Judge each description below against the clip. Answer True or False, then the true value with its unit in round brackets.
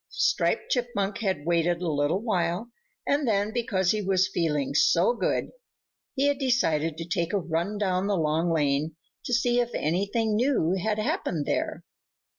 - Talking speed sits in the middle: True (165 wpm)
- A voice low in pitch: False (190 Hz)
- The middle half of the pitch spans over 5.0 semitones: True (5.5 semitones)